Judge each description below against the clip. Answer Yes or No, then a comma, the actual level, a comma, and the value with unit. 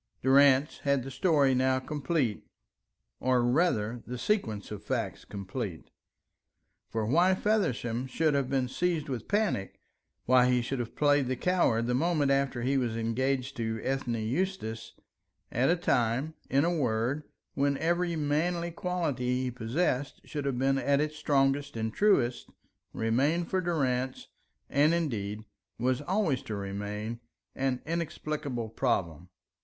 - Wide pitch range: No, average, 4.5 semitones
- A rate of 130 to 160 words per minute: Yes, average, 140 wpm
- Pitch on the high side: No, low, 135 Hz